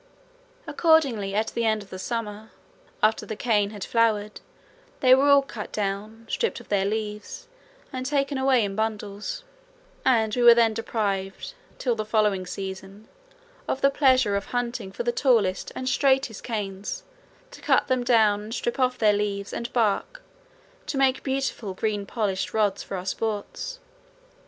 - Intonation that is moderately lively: Yes, average, 3.8 semitones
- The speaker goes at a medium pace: Yes, average, 160 wpm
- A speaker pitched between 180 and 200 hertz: No, high, 220 Hz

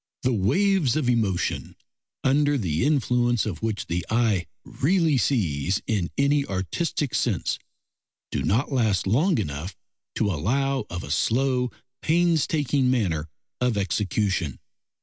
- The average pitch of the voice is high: No, low, 120 Hz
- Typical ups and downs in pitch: No, wide, 6.6 semitones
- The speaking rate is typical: No, slow, 125 wpm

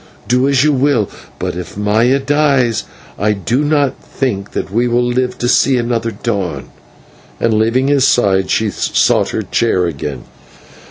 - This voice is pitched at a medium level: No, low, 120 Hz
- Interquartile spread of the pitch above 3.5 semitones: Yes, average, 4.4 semitones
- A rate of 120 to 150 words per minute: No, average, 160 wpm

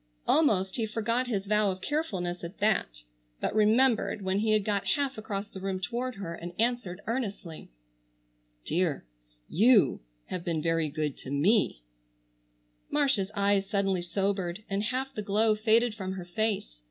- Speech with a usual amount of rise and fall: Yes, average, 3.5 semitones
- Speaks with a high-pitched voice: Yes, high, 200 Hz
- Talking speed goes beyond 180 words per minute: No, average, 155 wpm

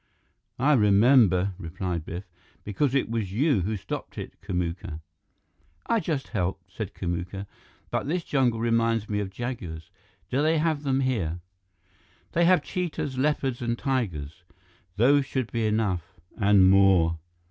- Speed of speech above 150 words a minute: No, average, 140 wpm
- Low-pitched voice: Yes, low, 110 Hz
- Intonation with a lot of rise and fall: Yes, wide, 6.2 semitones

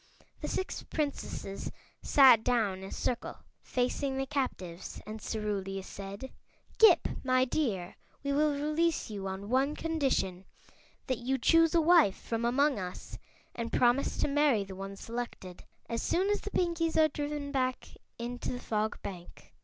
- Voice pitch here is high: Yes, very high, 250 Hz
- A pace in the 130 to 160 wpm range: Yes, average, 155 wpm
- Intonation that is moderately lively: No, wide, 6.5 semitones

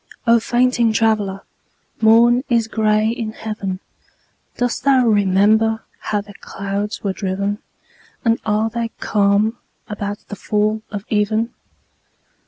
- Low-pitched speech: No, high, 215 Hz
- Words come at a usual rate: No, slow, 120 wpm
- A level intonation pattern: Yes, narrow, 1.9 semitones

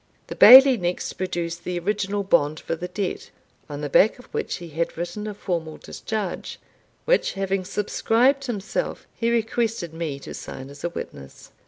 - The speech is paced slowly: No, average, 170 wpm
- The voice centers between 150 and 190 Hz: Yes, medium, 185 Hz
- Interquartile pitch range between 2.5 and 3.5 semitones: No, average, 4.3 semitones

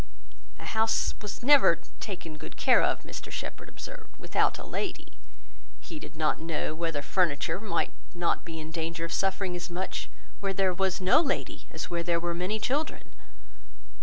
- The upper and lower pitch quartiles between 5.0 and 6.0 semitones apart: No, average, 3.9 semitones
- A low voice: No, medium, 180 Hz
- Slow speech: No, average, 170 wpm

